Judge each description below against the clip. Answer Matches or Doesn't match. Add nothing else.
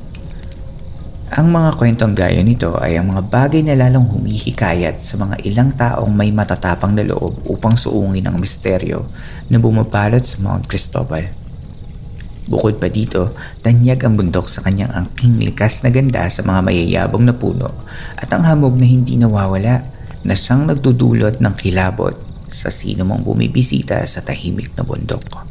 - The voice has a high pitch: Doesn't match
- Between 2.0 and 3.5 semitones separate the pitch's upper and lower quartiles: Doesn't match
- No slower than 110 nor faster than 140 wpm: Doesn't match